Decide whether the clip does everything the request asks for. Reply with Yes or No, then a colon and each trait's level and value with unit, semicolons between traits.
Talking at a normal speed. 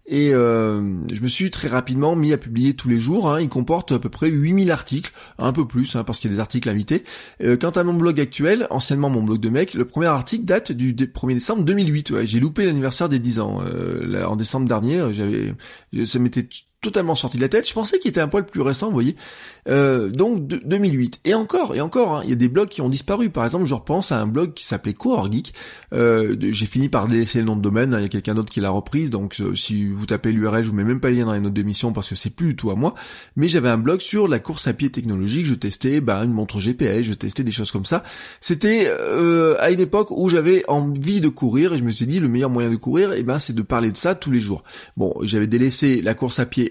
No: fast, 270 wpm